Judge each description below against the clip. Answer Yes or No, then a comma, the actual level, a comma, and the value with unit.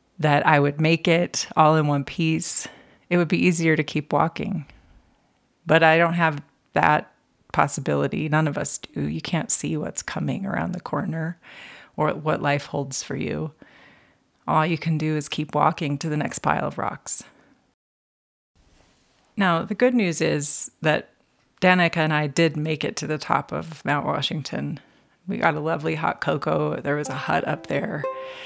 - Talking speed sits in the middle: Yes, average, 175 wpm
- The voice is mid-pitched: Yes, medium, 155 Hz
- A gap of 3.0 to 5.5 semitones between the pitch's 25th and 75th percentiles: No, narrow, 2.4 semitones